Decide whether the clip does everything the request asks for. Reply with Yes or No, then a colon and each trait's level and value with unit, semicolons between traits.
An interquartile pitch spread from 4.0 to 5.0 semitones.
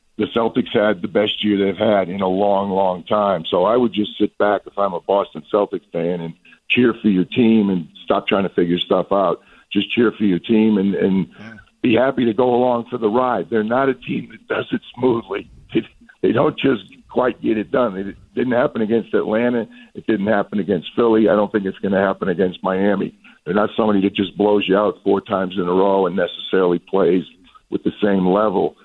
No: average, 2.9 semitones